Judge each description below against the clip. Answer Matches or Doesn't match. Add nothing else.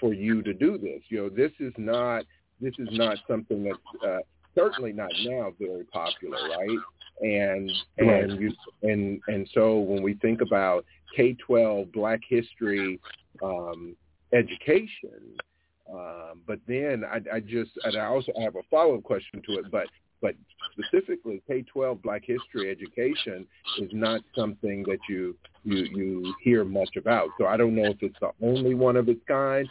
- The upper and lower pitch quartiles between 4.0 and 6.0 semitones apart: Doesn't match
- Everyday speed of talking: Matches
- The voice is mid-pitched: Doesn't match